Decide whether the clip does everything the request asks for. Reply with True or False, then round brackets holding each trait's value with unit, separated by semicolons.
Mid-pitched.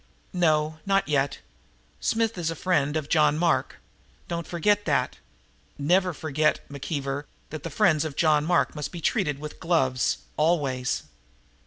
True (155 Hz)